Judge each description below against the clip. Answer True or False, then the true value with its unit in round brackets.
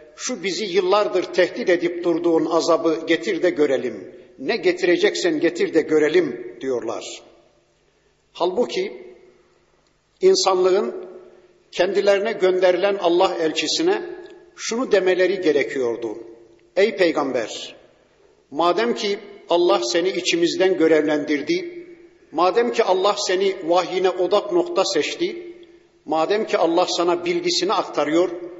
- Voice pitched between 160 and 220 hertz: True (190 Hz)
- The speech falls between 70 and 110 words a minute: True (100 wpm)